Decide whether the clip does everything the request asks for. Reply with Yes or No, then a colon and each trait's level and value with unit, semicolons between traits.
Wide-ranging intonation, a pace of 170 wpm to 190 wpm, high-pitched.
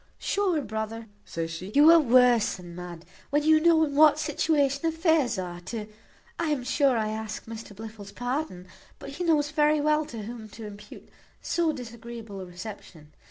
Yes: wide, 6.4 semitones; average, 175 wpm; high, 240 Hz